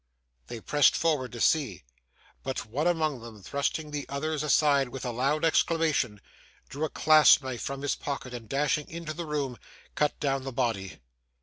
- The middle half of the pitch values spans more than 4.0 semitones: No, average, 3.6 semitones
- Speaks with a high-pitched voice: No, medium, 140 Hz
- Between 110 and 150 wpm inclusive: No, average, 175 wpm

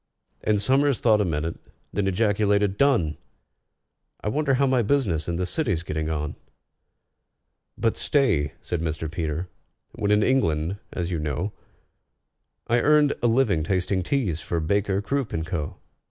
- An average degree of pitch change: No, wide, 6.6 semitones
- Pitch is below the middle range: Yes, low, 100 Hz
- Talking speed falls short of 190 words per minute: Yes, average, 150 wpm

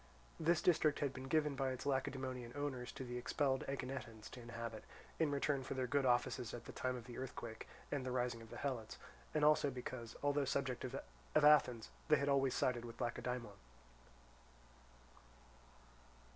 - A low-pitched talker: Yes, low, 130 Hz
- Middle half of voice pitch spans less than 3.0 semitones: Yes, narrow, 2.6 semitones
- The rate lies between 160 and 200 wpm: Yes, average, 170 wpm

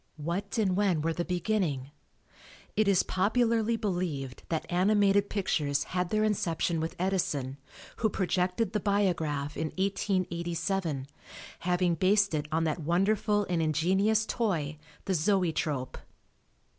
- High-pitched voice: No, medium, 180 Hz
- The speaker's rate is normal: No, slow, 125 wpm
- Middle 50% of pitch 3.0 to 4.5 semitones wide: Yes, average, 4.0 semitones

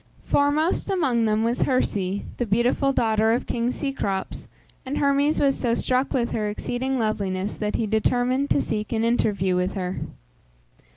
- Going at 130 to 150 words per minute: No, average, 160 wpm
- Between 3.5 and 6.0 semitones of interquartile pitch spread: Yes, average, 4.1 semitones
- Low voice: No, high, 235 Hz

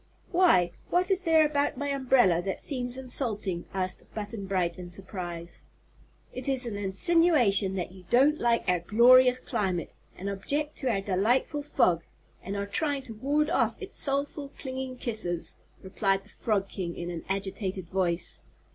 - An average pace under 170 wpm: Yes, average, 160 wpm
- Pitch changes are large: Yes, wide, 6.4 semitones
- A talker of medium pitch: No, high, 215 Hz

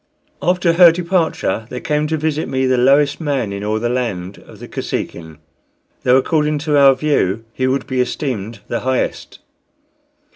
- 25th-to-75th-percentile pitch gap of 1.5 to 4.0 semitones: No, average, 4.4 semitones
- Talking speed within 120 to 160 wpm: No, average, 170 wpm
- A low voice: Yes, low, 130 Hz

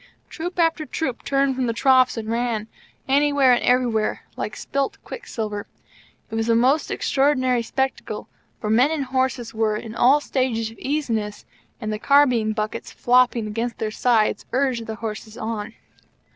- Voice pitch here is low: No, high, 245 Hz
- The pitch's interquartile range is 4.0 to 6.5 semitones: No, average, 3.3 semitones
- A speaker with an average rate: Yes, average, 160 wpm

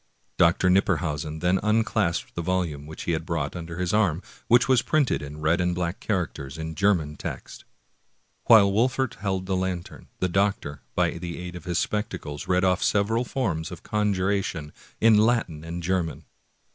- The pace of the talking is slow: No, average, 170 wpm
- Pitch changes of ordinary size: Yes, average, 3.8 semitones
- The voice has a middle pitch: No, very low, 90 Hz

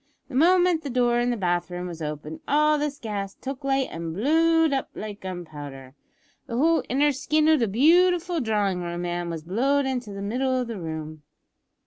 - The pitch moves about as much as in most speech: No, wide, 8.7 semitones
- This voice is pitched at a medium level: No, high, 240 Hz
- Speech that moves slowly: No, average, 190 wpm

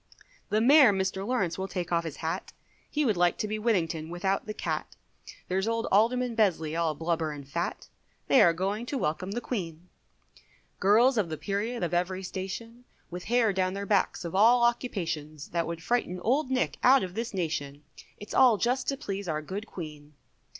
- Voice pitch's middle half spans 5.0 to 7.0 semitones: Yes, average, 5.3 semitones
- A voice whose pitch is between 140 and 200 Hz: Yes, high, 190 Hz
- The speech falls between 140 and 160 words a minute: No, average, 190 wpm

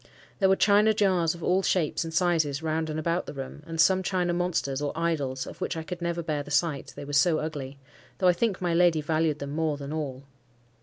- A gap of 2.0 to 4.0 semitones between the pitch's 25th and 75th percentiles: Yes, average, 3.3 semitones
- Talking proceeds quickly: Yes, fast, 235 wpm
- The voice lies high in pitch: No, medium, 160 Hz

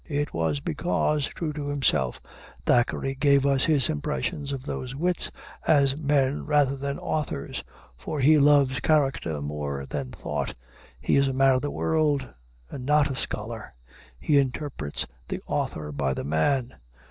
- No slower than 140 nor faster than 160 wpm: Yes, average, 155 wpm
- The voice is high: No, low, 135 Hz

